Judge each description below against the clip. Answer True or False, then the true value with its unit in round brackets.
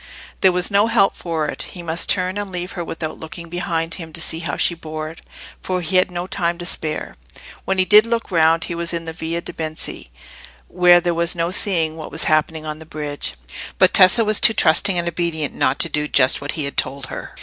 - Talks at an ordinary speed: False (235 wpm)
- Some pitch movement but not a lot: False (2.3 semitones)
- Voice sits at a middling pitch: True (170 Hz)